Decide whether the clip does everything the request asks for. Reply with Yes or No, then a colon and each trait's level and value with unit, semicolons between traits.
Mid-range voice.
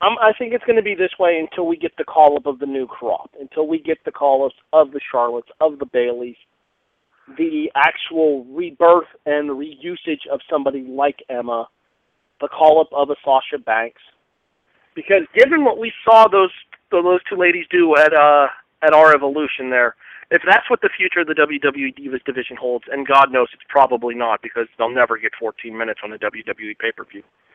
Yes: medium, 145 Hz